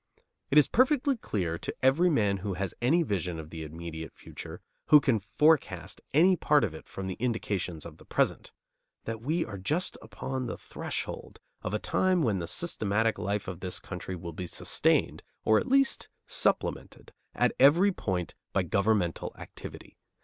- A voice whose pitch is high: No, low, 110 Hz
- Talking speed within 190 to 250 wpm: No, average, 170 wpm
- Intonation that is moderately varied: No, wide, 8.6 semitones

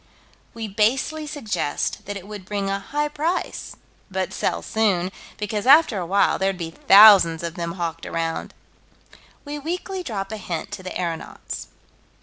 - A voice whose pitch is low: No, high, 200 Hz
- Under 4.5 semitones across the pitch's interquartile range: No, average, 4.8 semitones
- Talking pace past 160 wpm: No, average, 155 wpm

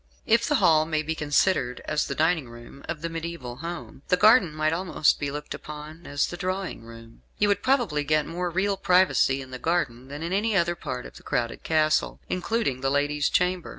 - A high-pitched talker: No, medium, 160 Hz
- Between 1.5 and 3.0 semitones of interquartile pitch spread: No, average, 4.1 semitones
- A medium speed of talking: No, fast, 210 wpm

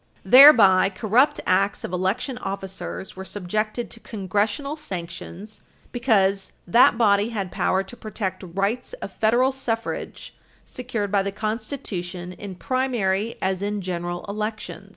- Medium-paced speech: No, slow, 130 wpm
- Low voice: No, high, 205 Hz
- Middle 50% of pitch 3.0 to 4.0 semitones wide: Yes, average, 3.5 semitones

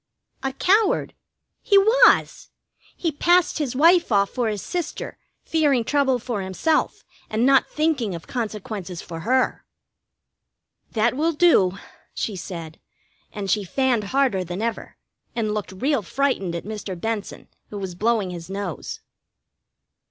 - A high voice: Yes, high, 230 Hz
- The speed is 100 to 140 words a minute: Yes, slow, 135 wpm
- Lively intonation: Yes, wide, 6.5 semitones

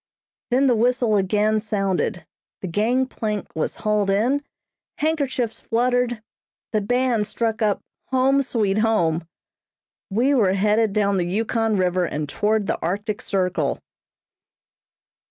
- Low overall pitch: No, high, 215 Hz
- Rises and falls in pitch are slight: No, average, 3.7 semitones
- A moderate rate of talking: No, slow, 120 wpm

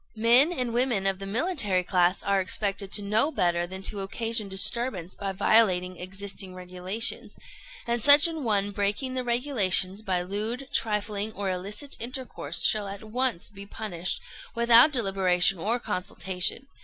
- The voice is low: No, high, 200 Hz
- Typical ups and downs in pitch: Yes, average, 3.9 semitones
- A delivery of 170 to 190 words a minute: No, average, 150 wpm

